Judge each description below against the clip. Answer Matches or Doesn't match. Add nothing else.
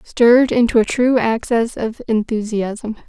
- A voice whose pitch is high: Matches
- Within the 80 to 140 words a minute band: Matches